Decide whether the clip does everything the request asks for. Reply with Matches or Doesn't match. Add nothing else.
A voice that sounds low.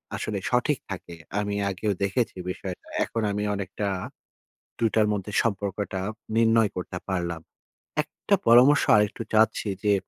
Matches